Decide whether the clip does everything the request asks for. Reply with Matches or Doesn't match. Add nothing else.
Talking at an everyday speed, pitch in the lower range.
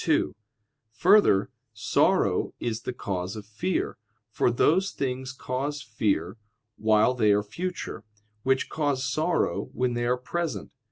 Doesn't match